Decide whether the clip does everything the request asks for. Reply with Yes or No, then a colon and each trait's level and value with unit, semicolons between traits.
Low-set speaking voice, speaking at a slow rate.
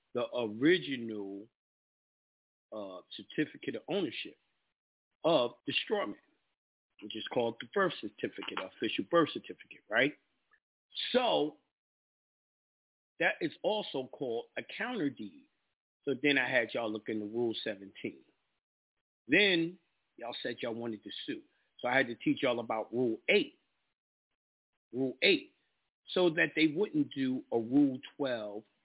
Yes: low, 125 Hz; slow, 130 wpm